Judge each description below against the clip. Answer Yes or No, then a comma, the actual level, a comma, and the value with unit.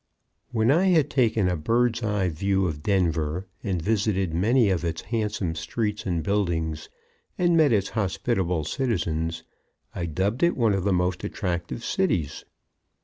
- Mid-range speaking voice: No, very low, 95 Hz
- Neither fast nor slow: Yes, average, 155 wpm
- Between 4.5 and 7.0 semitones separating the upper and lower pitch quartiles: Yes, average, 5.0 semitones